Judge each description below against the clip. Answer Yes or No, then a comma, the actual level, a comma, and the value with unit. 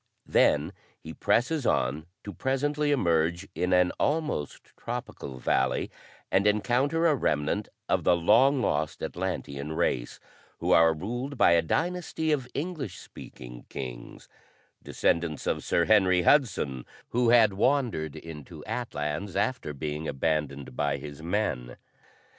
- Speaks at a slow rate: Yes, slow, 130 wpm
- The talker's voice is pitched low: Yes, very low, 90 Hz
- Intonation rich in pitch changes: Yes, wide, 8.8 semitones